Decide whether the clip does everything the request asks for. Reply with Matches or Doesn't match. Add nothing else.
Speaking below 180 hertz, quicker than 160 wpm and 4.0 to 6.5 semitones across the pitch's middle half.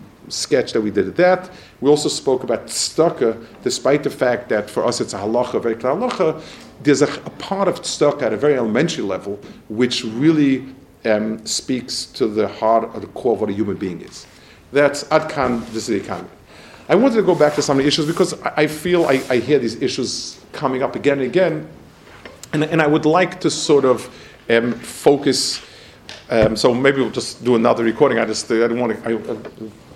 Matches